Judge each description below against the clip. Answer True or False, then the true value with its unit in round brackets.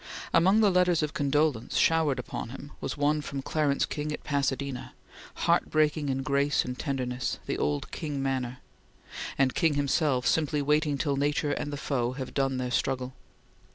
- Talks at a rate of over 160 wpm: True (170 wpm)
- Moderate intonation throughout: False (2.3 semitones)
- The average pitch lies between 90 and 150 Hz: True (140 Hz)